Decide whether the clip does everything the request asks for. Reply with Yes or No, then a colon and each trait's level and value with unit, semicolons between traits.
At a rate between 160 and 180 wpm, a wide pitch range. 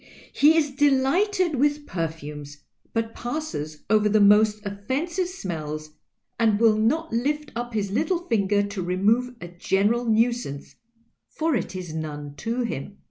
No: average, 140 wpm; wide, 6.9 semitones